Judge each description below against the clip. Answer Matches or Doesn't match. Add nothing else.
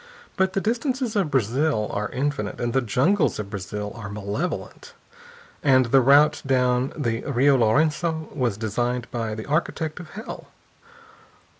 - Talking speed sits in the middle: Matches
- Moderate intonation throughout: Doesn't match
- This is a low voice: Matches